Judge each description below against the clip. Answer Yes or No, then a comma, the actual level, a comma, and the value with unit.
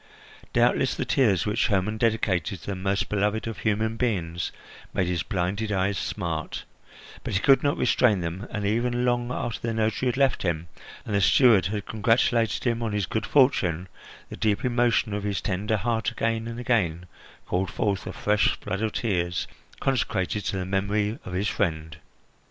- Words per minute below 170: No, average, 180 wpm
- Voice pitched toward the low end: Yes, low, 105 Hz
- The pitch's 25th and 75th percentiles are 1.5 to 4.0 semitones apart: Yes, average, 3.5 semitones